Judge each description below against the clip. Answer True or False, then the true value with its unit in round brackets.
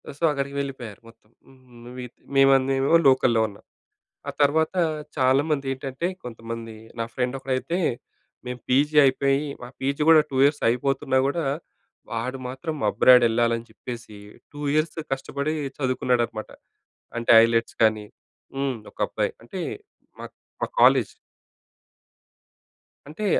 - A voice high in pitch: False (130 Hz)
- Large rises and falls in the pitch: False (2.9 semitones)